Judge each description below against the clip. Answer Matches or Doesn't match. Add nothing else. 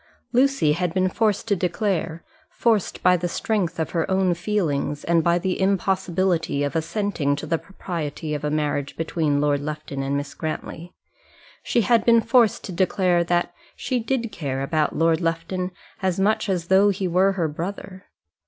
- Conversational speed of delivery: Matches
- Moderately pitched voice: Matches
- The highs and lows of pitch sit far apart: Doesn't match